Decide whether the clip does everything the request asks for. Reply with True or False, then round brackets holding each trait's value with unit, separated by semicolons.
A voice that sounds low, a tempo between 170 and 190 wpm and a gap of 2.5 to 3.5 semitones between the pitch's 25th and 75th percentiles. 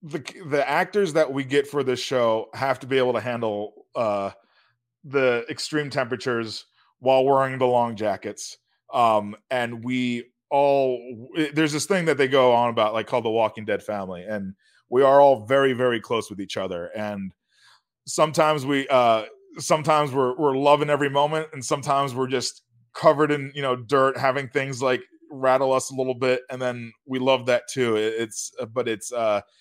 True (130 Hz; 185 wpm; 3.1 semitones)